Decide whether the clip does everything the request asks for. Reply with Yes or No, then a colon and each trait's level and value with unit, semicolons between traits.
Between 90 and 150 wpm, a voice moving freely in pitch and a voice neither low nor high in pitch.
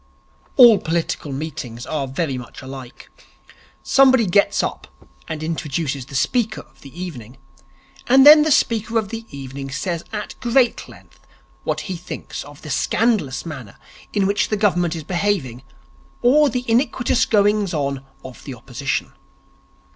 Yes: average, 145 wpm; wide, 8.5 semitones; medium, 170 Hz